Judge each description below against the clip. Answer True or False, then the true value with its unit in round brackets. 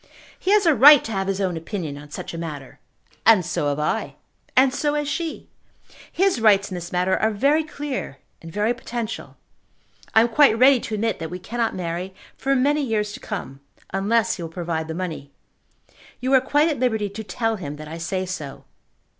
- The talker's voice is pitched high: True (210 Hz)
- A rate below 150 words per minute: False (205 wpm)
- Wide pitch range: True (7.0 semitones)